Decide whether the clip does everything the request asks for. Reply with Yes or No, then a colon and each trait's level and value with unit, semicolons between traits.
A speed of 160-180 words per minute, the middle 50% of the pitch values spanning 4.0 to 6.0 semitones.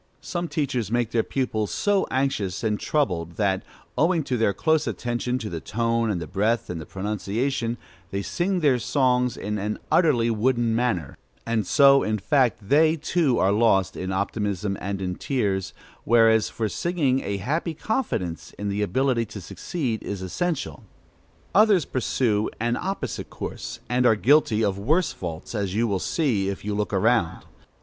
Yes: average, 170 wpm; average, 5.2 semitones